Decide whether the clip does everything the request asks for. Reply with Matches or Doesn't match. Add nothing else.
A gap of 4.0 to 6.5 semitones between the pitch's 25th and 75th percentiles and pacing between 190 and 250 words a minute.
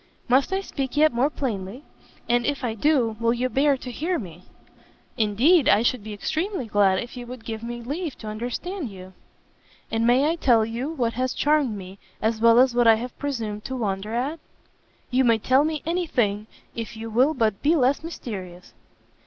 Matches